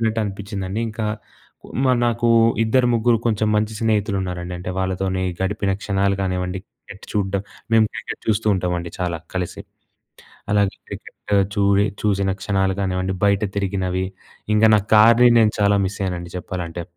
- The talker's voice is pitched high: No, low, 100 Hz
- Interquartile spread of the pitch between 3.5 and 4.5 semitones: No, narrow, 2.4 semitones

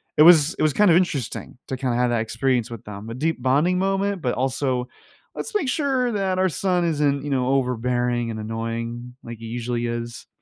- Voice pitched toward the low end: Yes, low, 130 Hz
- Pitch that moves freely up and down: Yes, wide, 6.4 semitones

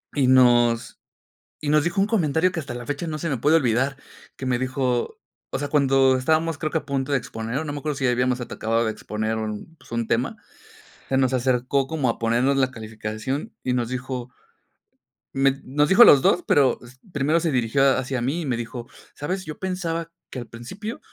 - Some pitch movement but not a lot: Yes, average, 3.9 semitones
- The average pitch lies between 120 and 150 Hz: Yes, low, 135 Hz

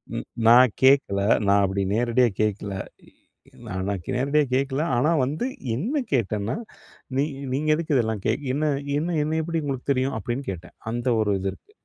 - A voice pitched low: Yes, low, 130 Hz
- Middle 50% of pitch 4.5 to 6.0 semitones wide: Yes, wide, 5.6 semitones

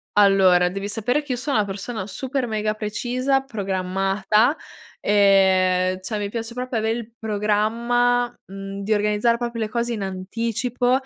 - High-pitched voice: Yes, high, 215 Hz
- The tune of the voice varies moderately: Yes, average, 3.5 semitones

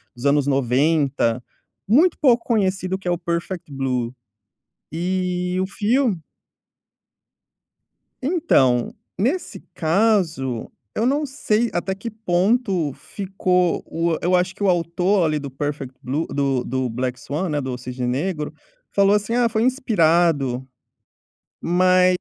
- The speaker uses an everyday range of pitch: No, wide, 6.3 semitones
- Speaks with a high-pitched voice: No, medium, 175 Hz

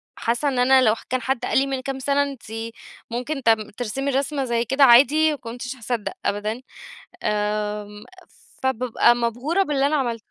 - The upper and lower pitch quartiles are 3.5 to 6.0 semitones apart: No, average, 3.0 semitones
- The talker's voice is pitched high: Yes, very high, 250 Hz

